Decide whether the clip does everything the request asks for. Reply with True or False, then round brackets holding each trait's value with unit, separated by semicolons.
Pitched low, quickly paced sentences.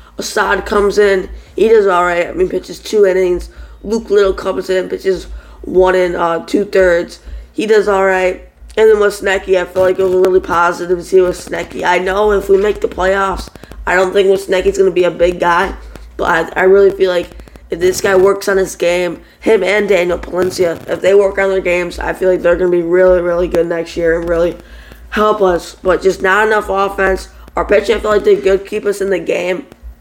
False (185 Hz; 230 wpm)